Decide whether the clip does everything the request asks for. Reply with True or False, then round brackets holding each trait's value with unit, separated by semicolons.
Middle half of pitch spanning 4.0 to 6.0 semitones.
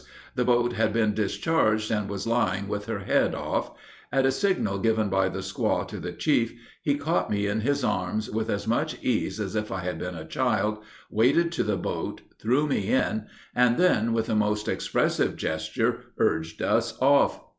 False (3.5 semitones)